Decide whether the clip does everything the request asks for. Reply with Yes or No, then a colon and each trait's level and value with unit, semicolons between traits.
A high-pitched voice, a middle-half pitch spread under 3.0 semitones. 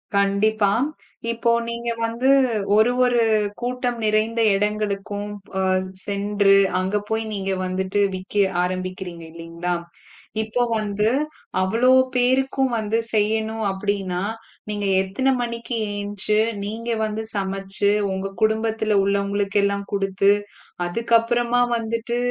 Yes: high, 210 Hz; narrow, 2.6 semitones